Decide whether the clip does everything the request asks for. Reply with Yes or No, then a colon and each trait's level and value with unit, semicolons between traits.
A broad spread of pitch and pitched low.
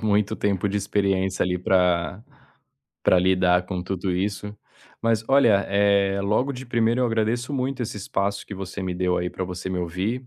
No: average, 3.2 semitones; low, 100 Hz